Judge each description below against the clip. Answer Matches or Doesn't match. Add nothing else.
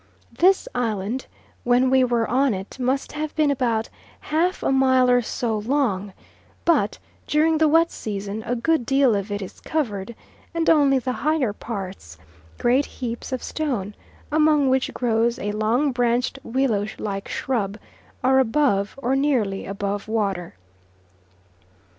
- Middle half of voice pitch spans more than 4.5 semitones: Matches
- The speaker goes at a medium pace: Matches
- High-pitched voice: Matches